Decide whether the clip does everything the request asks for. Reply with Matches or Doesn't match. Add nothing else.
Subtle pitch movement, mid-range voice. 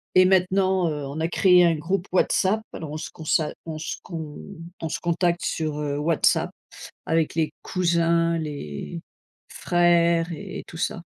Matches